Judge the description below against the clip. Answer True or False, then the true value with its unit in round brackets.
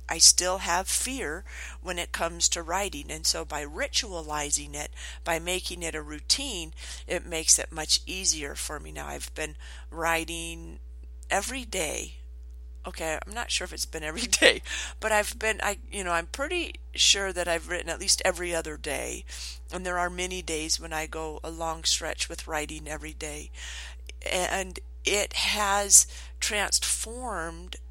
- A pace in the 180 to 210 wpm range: False (165 wpm)